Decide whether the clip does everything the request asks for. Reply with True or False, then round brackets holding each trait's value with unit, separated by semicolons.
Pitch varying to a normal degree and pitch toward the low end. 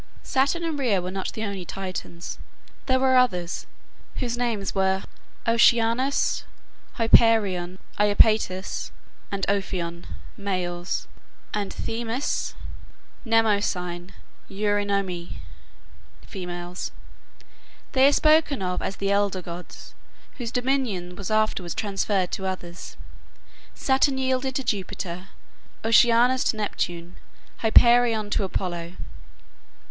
False (4.5 semitones; 205 Hz)